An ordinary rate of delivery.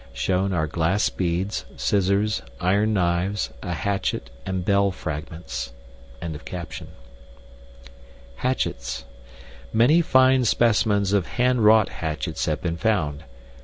No: slow, 95 wpm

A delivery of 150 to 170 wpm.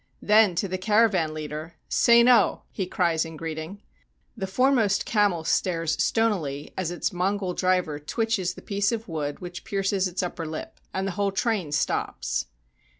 Yes: average, 160 wpm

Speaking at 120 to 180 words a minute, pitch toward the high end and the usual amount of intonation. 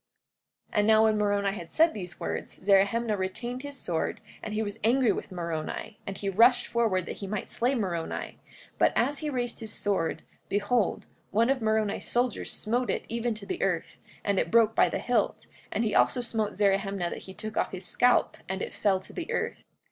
No: fast, 205 wpm; high, 215 Hz; average, 3.3 semitones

